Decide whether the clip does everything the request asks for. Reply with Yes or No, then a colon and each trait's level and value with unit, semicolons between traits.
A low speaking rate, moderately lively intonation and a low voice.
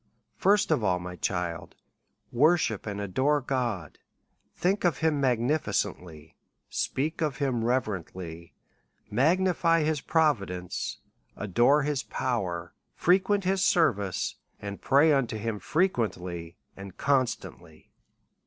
No: slow, 115 wpm; wide, 8.7 semitones; low, 125 Hz